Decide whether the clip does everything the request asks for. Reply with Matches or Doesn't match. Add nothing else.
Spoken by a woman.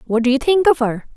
Matches